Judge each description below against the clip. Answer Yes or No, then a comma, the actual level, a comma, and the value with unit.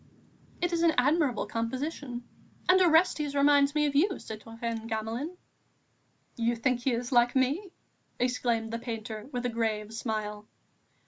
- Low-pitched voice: No, high, 245 Hz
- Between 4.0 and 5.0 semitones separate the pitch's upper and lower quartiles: Yes, average, 4.3 semitones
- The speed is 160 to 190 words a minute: No, average, 140 wpm